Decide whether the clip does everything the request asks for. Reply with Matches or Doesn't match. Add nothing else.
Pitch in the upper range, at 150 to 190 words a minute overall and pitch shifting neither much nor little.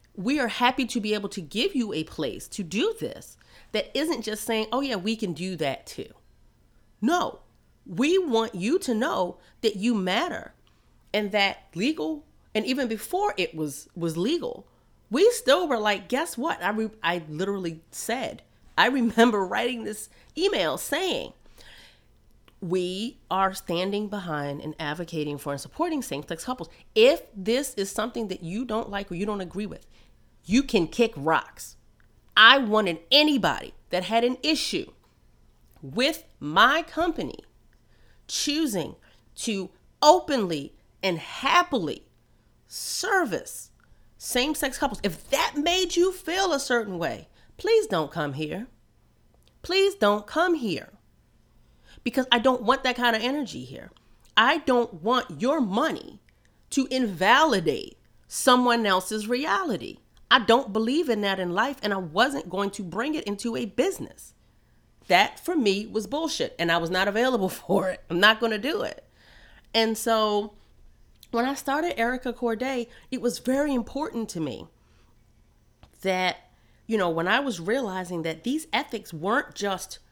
Doesn't match